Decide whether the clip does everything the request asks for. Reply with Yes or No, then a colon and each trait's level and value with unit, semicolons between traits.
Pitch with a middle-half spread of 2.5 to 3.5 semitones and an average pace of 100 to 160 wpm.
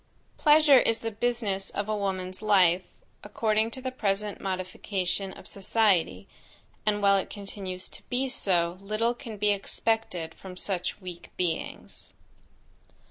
Yes: average, 3.2 semitones; slow, 135 wpm